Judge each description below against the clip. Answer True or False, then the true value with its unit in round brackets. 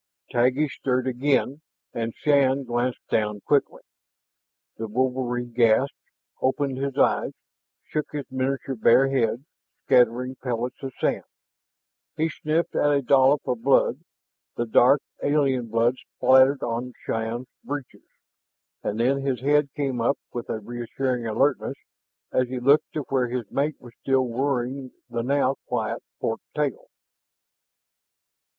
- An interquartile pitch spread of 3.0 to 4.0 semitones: False (2.4 semitones)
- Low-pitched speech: True (130 Hz)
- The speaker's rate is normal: False (130 wpm)